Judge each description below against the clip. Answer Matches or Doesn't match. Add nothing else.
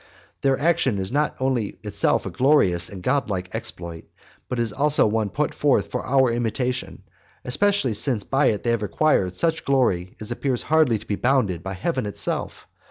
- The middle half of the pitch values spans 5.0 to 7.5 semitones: Matches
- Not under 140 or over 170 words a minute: Doesn't match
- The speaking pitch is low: Matches